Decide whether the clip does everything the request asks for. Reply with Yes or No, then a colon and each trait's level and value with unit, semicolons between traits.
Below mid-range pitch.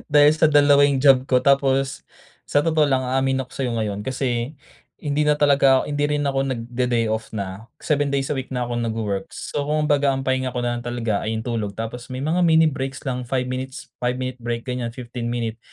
Yes: low, 130 Hz